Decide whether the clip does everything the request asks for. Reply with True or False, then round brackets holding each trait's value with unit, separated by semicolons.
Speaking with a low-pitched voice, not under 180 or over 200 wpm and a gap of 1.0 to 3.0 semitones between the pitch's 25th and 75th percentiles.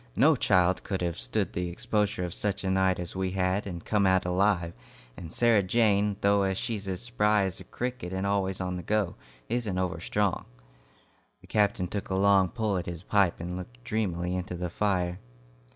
True (95 Hz; 195 wpm; 2.4 semitones)